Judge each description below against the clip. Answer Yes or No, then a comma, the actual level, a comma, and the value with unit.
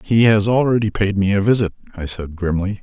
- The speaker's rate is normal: No, fast, 210 wpm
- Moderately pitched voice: No, low, 100 Hz